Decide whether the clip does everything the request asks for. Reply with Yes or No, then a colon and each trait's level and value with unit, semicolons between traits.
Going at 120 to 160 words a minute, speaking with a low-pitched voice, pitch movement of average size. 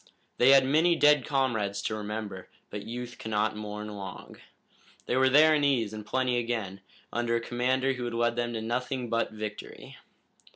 No: average, 175 wpm; low, 120 Hz; average, 3.5 semitones